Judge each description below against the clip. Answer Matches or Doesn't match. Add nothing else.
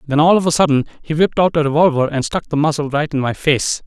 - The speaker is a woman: Doesn't match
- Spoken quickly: Matches